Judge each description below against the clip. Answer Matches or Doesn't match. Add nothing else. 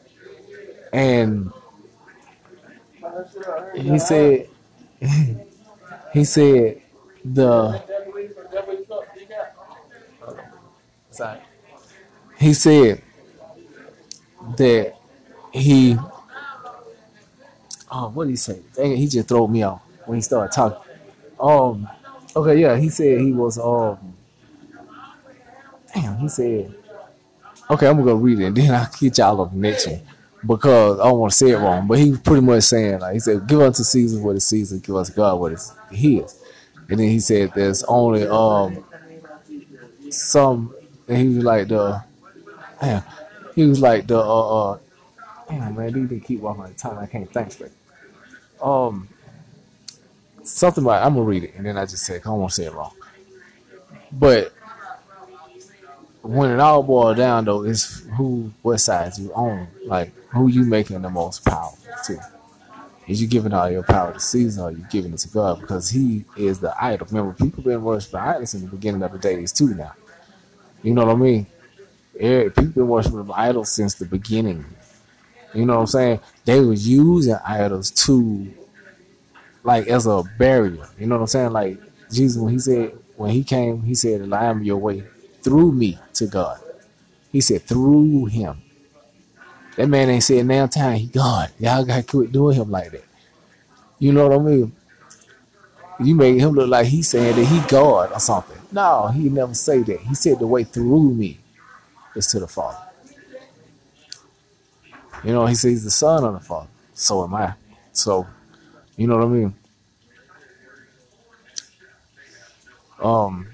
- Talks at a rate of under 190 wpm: Matches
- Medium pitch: Doesn't match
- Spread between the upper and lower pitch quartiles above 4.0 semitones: Matches